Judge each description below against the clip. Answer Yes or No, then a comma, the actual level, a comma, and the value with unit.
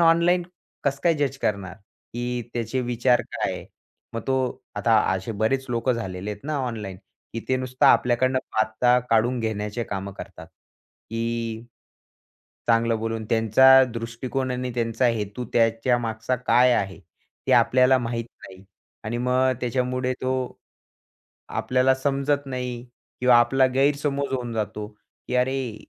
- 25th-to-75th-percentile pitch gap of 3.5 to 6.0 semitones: No, narrow, 2.5 semitones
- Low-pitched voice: Yes, low, 120 Hz